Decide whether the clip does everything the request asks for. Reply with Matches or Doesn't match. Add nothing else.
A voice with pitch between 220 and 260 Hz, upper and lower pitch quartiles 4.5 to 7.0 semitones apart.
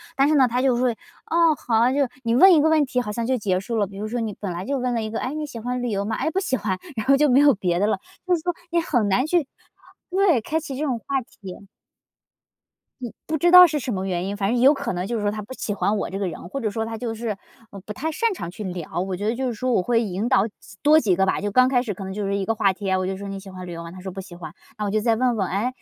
Matches